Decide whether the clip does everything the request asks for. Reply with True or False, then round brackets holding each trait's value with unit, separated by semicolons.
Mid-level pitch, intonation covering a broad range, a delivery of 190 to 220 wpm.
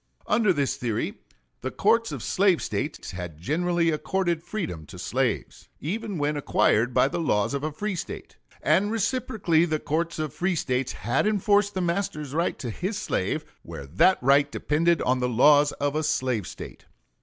False (155 Hz; 5.9 semitones; 175 wpm)